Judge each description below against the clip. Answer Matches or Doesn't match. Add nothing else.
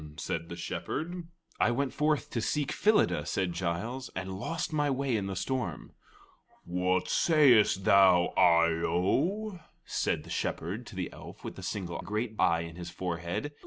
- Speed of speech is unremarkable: Matches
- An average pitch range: Doesn't match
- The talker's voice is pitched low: Matches